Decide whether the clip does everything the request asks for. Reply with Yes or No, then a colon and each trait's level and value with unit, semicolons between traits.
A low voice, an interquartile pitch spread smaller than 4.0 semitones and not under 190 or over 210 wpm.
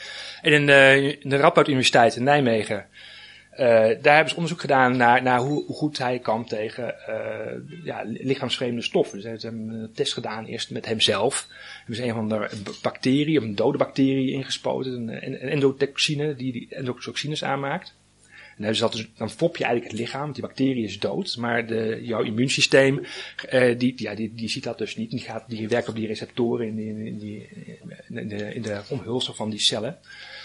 Yes: low, 125 Hz; average, 3.5 semitones; average, 195 wpm